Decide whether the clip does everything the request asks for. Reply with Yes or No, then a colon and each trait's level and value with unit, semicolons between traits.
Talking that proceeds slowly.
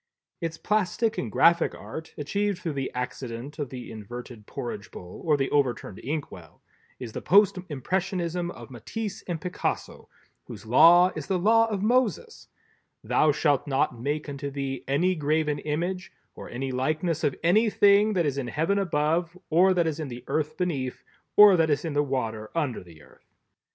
No: average, 170 wpm